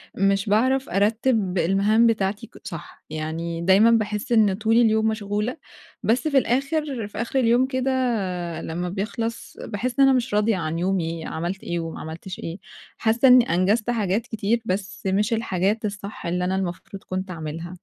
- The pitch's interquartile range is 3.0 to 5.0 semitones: Yes, average, 3.9 semitones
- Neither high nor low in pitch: No, high, 205 Hz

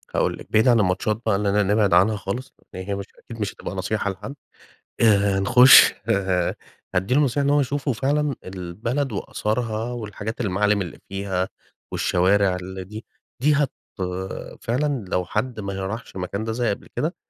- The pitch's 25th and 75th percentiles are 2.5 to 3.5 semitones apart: No, average, 4.0 semitones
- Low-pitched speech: Yes, low, 105 Hz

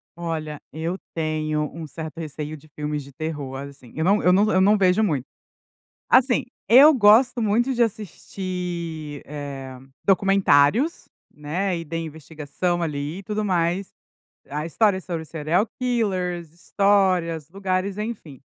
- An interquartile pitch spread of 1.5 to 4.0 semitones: No, average, 4.6 semitones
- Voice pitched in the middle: Yes, medium, 170 Hz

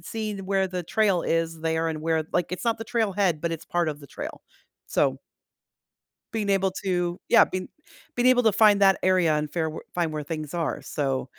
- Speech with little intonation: No, average, 3.6 semitones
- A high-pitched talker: No, medium, 175 Hz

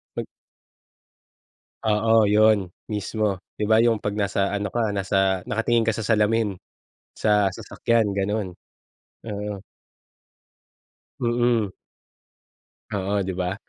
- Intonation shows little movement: Yes, narrow, 2.1 semitones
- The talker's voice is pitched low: Yes, low, 105 Hz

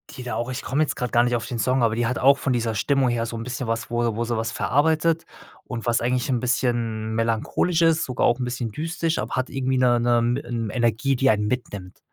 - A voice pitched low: Yes, low, 120 Hz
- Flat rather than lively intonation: Yes, narrow, 2.0 semitones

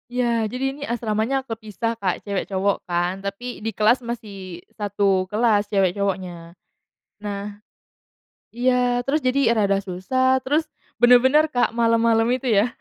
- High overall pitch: Yes, high, 225 Hz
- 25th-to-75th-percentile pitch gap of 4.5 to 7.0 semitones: No, average, 3.8 semitones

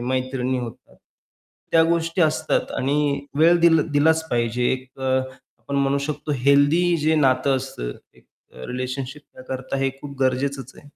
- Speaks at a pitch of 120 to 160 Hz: Yes, low, 135 Hz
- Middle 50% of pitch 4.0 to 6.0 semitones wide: No, average, 2.8 semitones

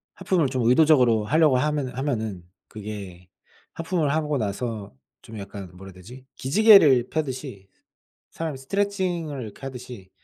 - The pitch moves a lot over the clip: Yes, wide, 6.4 semitones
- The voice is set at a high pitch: No, low, 130 Hz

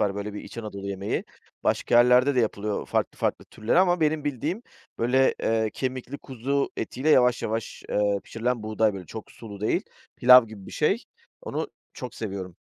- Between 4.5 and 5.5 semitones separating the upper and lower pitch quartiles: No, average, 3.9 semitones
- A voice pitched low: Yes, low, 115 Hz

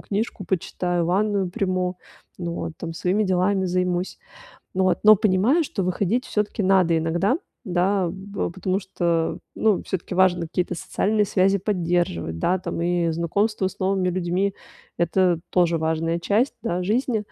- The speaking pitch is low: No, medium, 185 Hz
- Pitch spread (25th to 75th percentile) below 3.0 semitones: Yes, narrow, 2.4 semitones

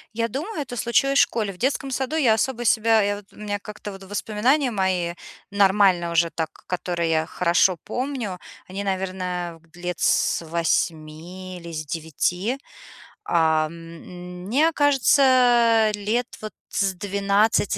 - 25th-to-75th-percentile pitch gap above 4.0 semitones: Yes, average, 5.0 semitones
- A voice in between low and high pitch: No, high, 200 Hz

